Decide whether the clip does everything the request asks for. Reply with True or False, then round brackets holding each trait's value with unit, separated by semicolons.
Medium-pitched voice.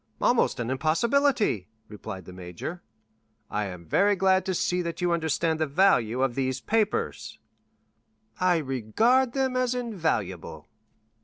True (160 Hz)